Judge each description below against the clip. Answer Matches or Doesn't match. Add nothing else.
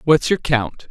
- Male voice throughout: Matches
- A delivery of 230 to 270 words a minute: Doesn't match